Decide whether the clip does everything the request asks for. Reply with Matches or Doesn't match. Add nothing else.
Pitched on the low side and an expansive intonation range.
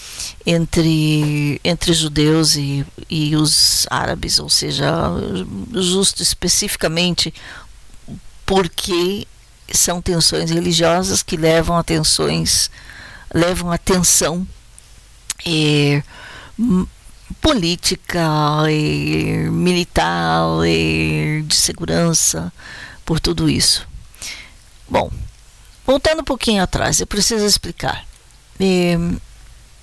Doesn't match